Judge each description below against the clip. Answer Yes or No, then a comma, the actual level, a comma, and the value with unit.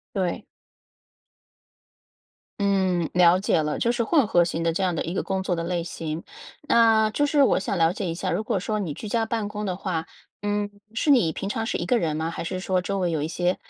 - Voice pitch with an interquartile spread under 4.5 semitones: Yes, average, 4.0 semitones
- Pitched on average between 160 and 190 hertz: Yes, medium, 185 Hz